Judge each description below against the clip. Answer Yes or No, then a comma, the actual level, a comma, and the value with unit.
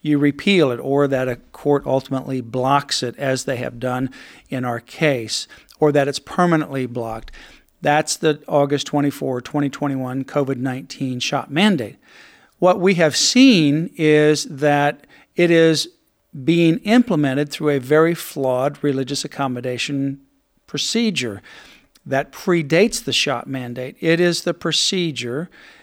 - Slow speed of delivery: Yes, slow, 130 wpm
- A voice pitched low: No, medium, 145 Hz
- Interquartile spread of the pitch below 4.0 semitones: Yes, average, 3.4 semitones